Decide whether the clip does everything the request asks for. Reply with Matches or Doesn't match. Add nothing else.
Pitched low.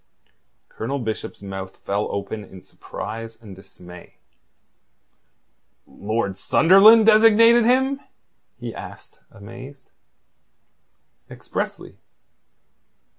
Matches